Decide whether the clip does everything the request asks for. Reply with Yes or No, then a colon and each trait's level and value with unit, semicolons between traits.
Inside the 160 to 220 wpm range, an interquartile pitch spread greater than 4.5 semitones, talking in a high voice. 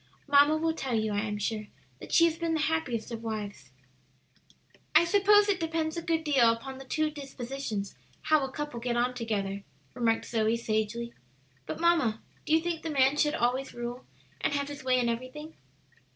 Yes: average, 190 wpm; wide, 5.4 semitones; very high, 265 Hz